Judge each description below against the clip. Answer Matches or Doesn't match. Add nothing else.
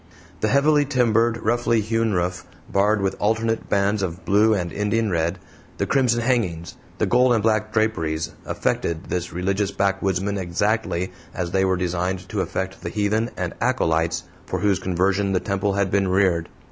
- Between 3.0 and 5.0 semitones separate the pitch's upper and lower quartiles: Matches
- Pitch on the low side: Matches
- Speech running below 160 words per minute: Doesn't match